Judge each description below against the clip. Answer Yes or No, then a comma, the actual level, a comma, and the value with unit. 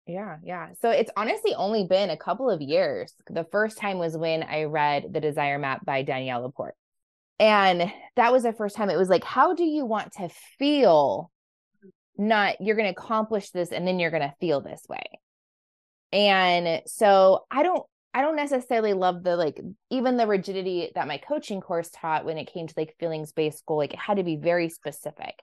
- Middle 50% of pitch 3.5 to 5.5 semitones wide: Yes, average, 4.8 semitones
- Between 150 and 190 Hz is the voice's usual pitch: Yes, medium, 185 Hz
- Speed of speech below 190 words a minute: No, average, 195 wpm